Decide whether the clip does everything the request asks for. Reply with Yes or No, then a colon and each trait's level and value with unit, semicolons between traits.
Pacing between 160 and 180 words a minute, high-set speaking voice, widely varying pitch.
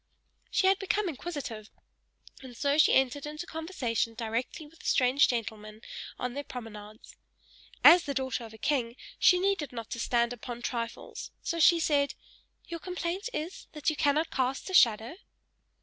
Yes: average, 165 wpm; very high, 275 Hz; wide, 5.8 semitones